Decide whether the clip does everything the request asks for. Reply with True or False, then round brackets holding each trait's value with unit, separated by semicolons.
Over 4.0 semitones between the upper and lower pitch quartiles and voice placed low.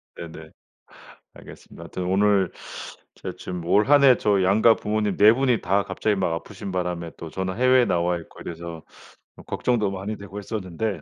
False (3.5 semitones; 100 Hz)